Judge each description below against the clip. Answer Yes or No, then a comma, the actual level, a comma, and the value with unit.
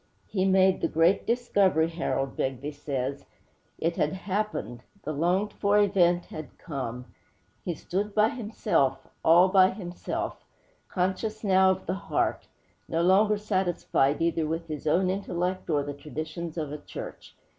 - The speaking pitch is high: No, medium, 175 Hz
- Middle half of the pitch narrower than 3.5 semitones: No, average, 4.0 semitones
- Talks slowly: No, average, 145 wpm